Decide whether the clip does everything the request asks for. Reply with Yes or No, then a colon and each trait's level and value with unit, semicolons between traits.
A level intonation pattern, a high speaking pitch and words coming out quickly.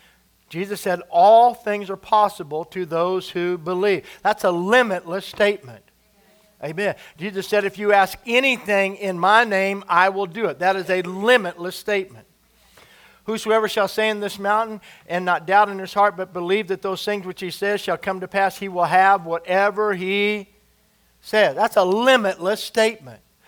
No: narrow, 2.1 semitones; high, 195 Hz; average, 170 wpm